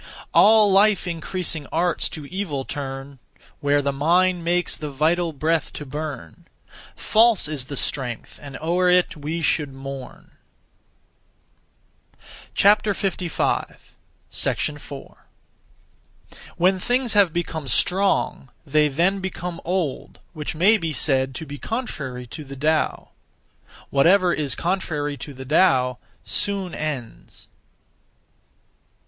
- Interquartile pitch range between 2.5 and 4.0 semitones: No, average, 4.6 semitones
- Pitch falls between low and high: Yes, medium, 160 Hz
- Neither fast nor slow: No, slow, 110 wpm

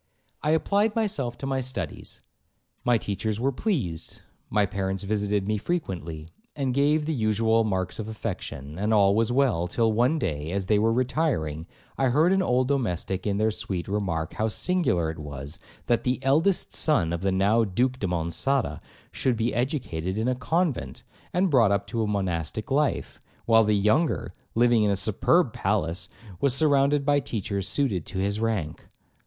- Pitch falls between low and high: No, low, 110 Hz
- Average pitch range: No, wide, 5.8 semitones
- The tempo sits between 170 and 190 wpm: Yes, average, 175 wpm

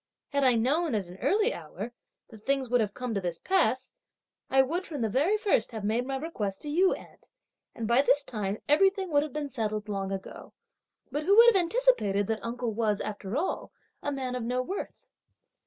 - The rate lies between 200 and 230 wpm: Yes, fast, 205 wpm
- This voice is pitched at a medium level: No, very high, 255 Hz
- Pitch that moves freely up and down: Yes, wide, 6.2 semitones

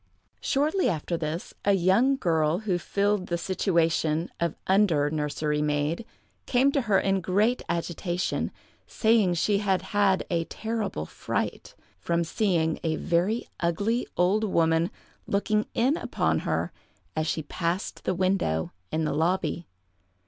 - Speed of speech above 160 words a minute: No, average, 140 wpm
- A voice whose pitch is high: No, medium, 180 Hz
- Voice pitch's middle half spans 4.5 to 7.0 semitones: No, average, 4.1 semitones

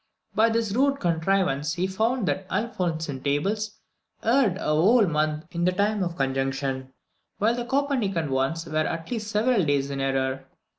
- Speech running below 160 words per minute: No, average, 165 wpm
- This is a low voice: No, medium, 175 Hz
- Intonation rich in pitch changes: Yes, wide, 6.8 semitones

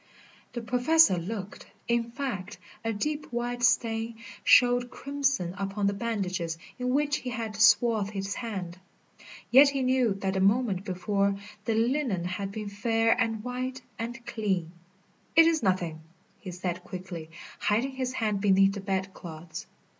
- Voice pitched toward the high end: Yes, high, 220 Hz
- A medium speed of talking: Yes, average, 150 wpm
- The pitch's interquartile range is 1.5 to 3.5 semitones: No, average, 4.3 semitones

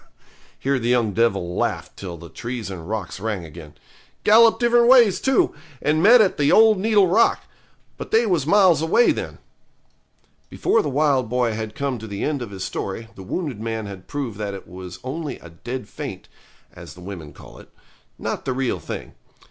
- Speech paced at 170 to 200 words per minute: Yes, average, 190 wpm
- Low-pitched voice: Yes, low, 125 Hz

